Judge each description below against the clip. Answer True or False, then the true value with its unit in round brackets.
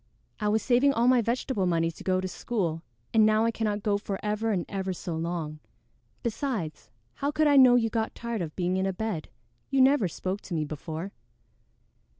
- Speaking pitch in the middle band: False (205 Hz)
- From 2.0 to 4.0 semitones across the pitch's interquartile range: False (4.9 semitones)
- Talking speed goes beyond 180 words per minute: True (200 wpm)